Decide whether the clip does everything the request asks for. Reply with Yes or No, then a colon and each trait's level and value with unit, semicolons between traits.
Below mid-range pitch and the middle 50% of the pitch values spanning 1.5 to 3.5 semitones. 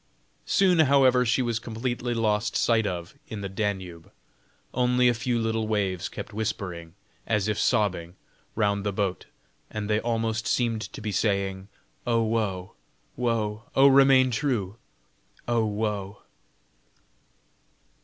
Yes: low, 110 Hz; average, 2.9 semitones